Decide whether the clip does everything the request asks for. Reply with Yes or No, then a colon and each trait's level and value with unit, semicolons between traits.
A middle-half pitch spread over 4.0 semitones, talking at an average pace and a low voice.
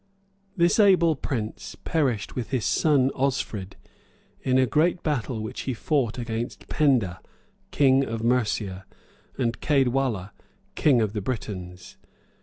No: average, 5.2 semitones; slow, 130 wpm; low, 130 Hz